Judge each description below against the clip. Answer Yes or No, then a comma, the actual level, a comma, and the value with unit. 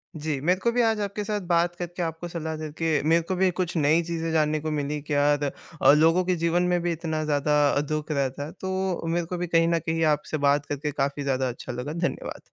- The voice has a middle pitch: Yes, medium, 160 Hz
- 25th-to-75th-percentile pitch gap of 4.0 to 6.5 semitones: No, average, 2.9 semitones